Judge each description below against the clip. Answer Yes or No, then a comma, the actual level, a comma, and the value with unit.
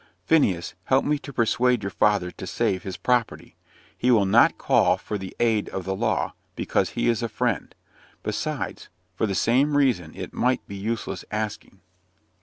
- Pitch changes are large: No, average, 4.3 semitones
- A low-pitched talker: Yes, low, 110 Hz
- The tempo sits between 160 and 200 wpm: Yes, average, 175 wpm